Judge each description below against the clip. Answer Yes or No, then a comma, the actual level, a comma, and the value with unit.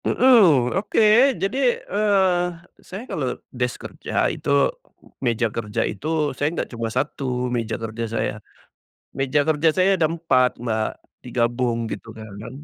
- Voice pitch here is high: No, low, 130 Hz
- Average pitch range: No, wide, 7.8 semitones